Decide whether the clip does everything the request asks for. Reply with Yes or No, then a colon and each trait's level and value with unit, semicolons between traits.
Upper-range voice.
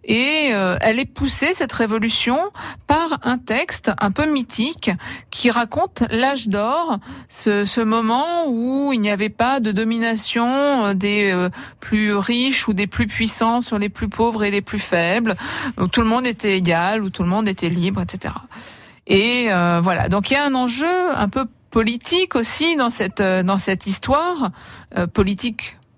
Yes: high, 225 Hz